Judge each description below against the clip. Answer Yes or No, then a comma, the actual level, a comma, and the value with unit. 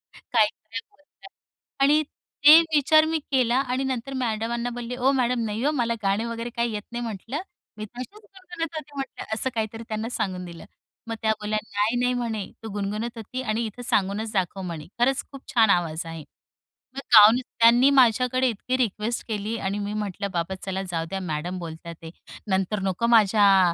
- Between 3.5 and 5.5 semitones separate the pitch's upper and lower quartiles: Yes, average, 4.0 semitones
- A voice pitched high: Yes, high, 225 Hz